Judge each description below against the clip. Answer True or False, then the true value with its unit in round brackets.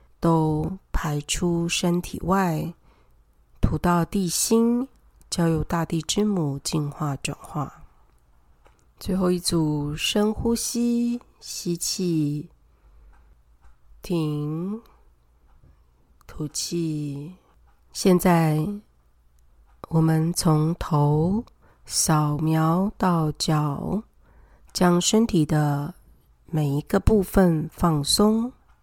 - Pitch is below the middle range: False (160 Hz)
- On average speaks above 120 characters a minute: False (110 characters per minute)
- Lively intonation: False (4.1 semitones)